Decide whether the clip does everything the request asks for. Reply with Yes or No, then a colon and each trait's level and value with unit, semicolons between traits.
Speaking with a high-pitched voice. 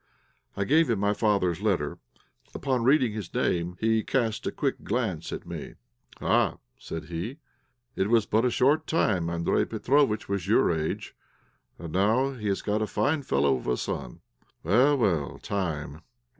No: low, 105 Hz